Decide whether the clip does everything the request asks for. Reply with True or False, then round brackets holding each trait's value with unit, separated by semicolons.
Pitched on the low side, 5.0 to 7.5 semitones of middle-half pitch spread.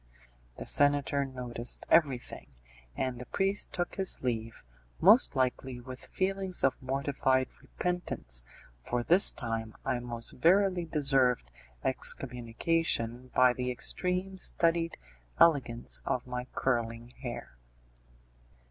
True (130 Hz; 5.6 semitones)